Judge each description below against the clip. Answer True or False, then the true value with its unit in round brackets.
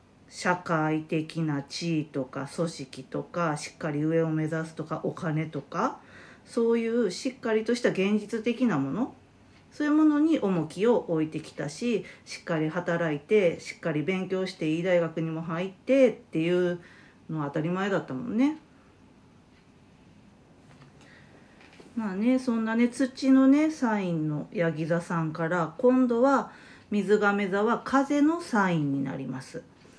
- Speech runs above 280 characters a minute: False (275 characters per minute)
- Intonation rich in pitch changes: True (6.5 semitones)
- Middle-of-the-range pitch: True (180 Hz)